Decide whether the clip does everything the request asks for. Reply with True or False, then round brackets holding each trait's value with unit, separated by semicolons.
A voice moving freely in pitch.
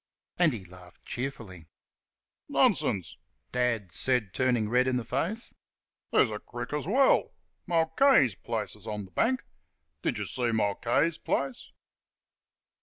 True (6.0 semitones)